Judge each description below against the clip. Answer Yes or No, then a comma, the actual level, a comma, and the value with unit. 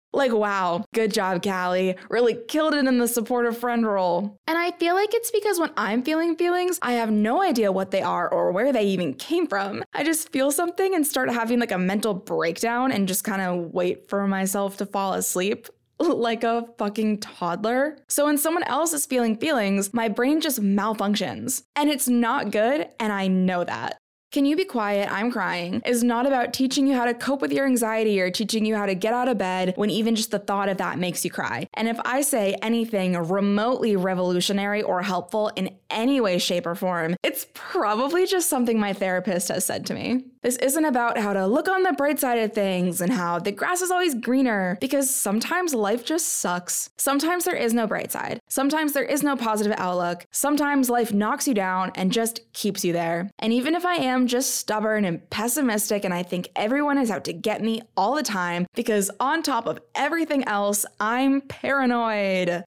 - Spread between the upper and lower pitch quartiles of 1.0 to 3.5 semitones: No, wide, 5.6 semitones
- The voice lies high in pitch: Yes, high, 225 Hz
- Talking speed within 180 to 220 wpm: Yes, fast, 205 wpm